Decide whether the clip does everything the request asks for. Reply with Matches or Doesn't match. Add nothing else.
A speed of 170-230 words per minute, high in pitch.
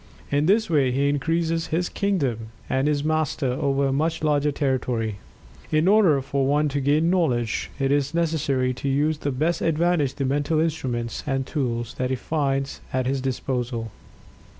Doesn't match